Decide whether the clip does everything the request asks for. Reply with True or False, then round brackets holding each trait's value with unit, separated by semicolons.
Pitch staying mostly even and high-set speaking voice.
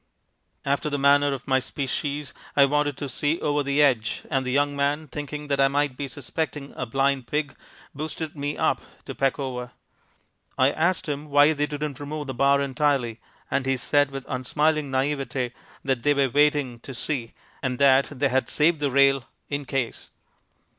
False (1.7 semitones; 140 Hz)